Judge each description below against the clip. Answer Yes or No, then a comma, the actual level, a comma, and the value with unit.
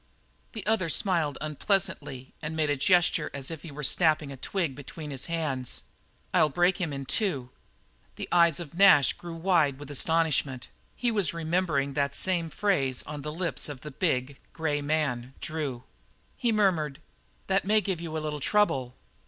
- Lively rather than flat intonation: No, average, 3.9 semitones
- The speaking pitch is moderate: Yes, medium, 155 Hz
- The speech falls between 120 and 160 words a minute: No, average, 170 wpm